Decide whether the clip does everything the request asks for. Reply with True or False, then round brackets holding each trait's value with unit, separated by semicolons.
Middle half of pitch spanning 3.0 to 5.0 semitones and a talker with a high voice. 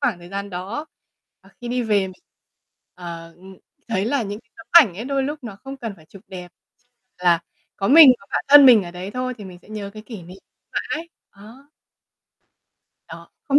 False (5.4 semitones; 205 Hz)